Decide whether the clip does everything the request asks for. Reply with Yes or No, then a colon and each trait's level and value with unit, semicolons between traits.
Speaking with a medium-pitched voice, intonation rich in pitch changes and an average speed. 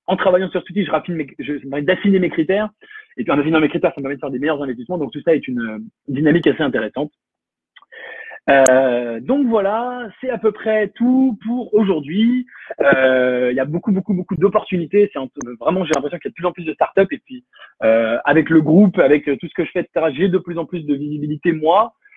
No: medium, 175 Hz; wide, 6.3 semitones; fast, 245 wpm